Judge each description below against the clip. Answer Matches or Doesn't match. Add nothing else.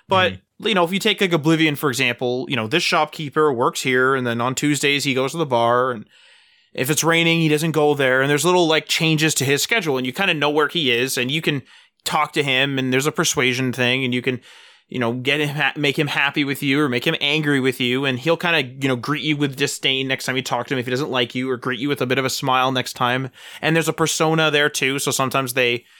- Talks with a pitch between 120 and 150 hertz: Matches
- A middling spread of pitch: Matches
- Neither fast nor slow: Doesn't match